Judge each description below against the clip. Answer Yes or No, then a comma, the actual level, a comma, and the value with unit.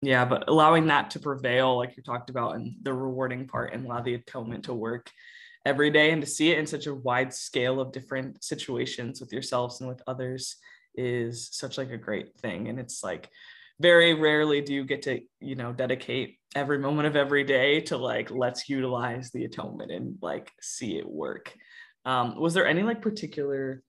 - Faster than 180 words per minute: Yes, average, 200 wpm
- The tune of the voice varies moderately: Yes, average, 3.0 semitones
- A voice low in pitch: Yes, low, 130 Hz